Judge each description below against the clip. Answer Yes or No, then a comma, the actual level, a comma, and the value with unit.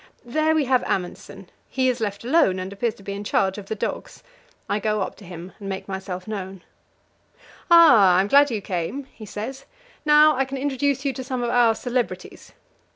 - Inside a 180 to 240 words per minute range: Yes, average, 200 wpm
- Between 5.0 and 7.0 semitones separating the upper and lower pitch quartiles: Yes, wide, 5.5 semitones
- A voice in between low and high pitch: No, high, 225 Hz